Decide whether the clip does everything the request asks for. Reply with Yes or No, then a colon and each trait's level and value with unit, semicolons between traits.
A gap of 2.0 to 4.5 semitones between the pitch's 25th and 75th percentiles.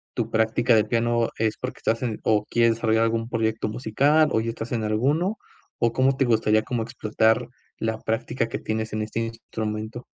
No: narrow, 1.4 semitones